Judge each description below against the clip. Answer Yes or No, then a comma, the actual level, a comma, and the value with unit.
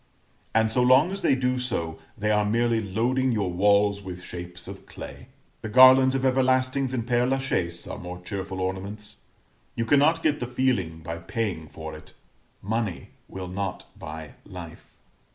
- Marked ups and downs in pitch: Yes, wide, 6.0 semitones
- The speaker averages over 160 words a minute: Yes, average, 170 wpm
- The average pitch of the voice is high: No, low, 105 Hz